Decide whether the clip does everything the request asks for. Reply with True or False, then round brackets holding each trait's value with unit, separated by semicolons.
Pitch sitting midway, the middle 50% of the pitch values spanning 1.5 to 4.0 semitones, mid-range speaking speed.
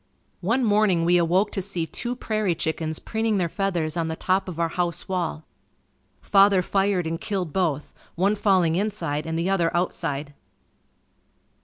True (180 Hz; 3.3 semitones; 160 wpm)